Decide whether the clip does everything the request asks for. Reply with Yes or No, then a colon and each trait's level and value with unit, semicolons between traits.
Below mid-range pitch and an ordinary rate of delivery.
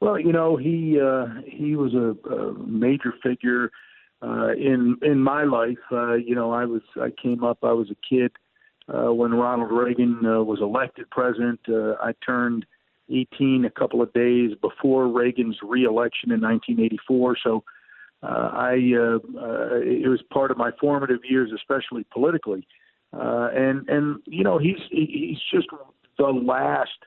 Yes: low, 125 Hz; average, 160 wpm